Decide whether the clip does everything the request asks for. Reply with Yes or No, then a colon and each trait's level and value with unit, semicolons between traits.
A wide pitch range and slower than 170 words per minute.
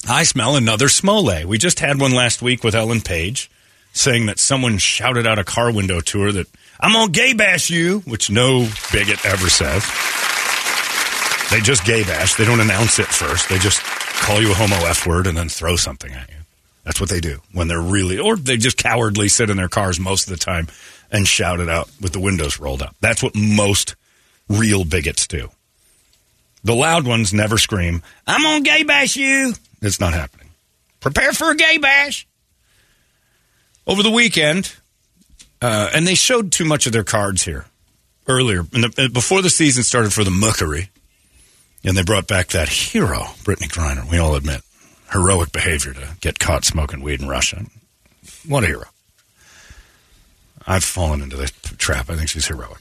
No: wide, 6.1 semitones; average, 185 wpm